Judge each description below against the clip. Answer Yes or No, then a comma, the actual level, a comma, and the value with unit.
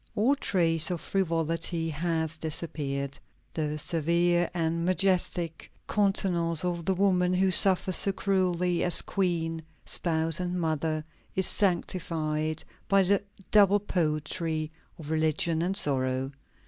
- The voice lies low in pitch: No, medium, 170 Hz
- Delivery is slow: Yes, slow, 120 wpm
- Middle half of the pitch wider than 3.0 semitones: No, narrow, 2.6 semitones